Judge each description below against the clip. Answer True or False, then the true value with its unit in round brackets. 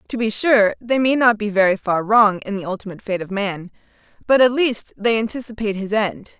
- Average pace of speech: False (215 wpm)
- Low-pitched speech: False (215 Hz)